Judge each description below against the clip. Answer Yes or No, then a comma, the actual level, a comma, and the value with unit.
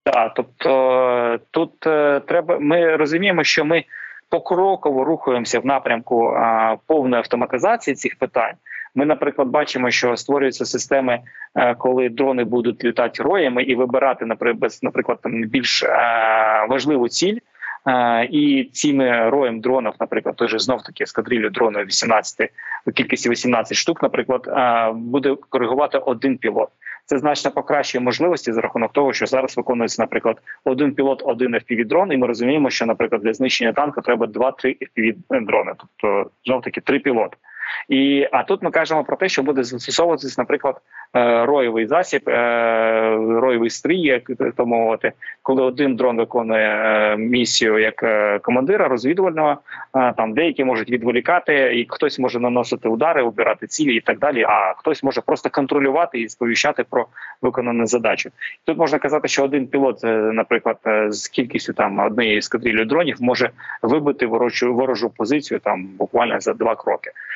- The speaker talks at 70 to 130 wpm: No, average, 145 wpm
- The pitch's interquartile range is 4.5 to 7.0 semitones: No, average, 3.8 semitones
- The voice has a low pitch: Yes, low, 130 Hz